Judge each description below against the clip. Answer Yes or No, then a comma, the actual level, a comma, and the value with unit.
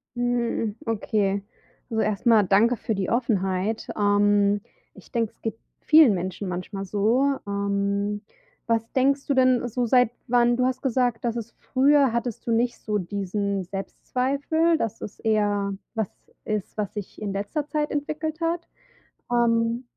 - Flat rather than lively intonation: No, average, 3.7 semitones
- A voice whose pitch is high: Yes, high, 225 Hz